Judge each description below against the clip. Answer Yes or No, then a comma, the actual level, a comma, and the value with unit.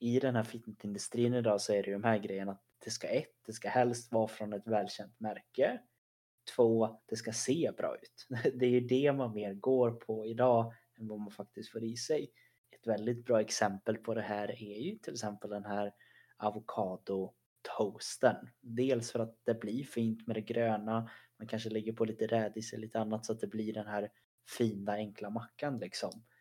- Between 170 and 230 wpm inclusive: Yes, fast, 195 wpm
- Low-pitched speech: Yes, low, 110 Hz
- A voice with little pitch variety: Yes, narrow, 1.9 semitones